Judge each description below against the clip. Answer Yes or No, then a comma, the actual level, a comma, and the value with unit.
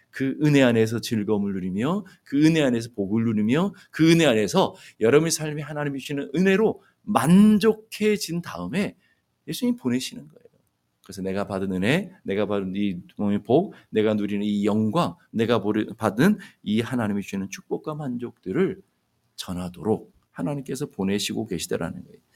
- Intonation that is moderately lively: No, wide, 7.6 semitones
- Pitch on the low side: Yes, low, 120 Hz